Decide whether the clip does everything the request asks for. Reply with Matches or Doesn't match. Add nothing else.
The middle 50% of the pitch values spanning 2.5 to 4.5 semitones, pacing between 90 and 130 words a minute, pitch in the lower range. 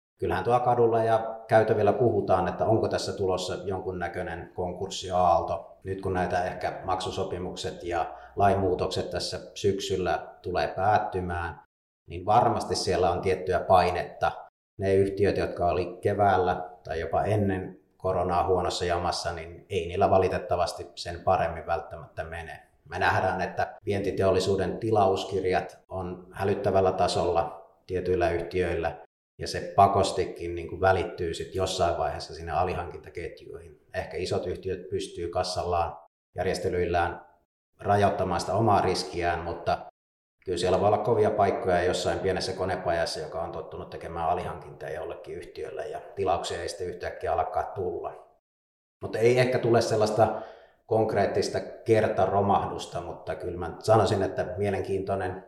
Doesn't match